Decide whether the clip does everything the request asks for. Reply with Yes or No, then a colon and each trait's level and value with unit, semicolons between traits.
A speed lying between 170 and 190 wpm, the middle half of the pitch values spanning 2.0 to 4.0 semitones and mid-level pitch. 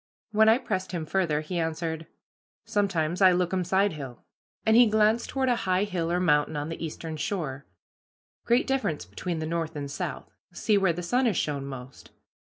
No: average, 180 wpm; average, 4.7 semitones; medium, 175 Hz